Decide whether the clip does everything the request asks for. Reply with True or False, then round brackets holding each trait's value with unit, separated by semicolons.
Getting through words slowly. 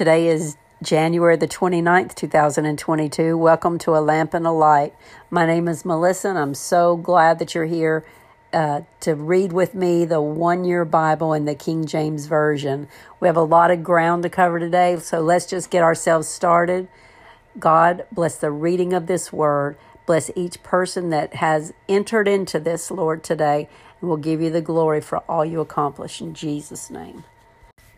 False (175 wpm)